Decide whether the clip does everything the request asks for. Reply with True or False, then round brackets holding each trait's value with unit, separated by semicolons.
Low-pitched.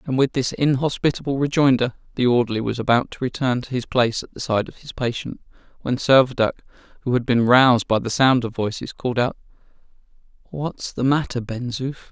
True (125 Hz)